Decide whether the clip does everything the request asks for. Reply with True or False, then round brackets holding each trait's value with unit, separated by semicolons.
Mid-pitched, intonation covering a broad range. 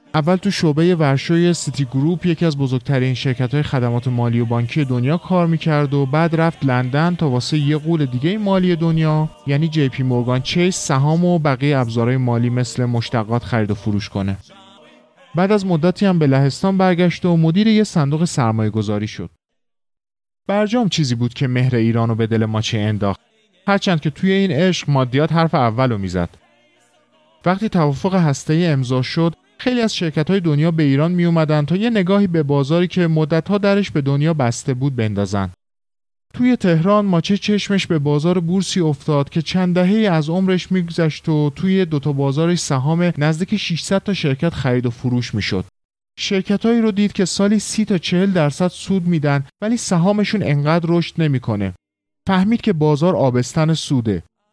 True (155 Hz; 6.0 semitones)